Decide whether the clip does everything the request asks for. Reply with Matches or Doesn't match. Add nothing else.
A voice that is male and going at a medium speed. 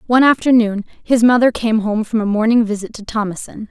Doesn't match